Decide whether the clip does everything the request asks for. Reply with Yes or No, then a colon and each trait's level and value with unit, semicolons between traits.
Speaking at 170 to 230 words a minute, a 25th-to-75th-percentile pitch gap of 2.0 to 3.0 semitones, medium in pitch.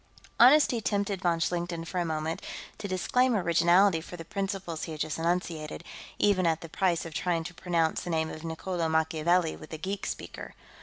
Yes: average, 190 wpm; narrow, 2.5 semitones; medium, 170 Hz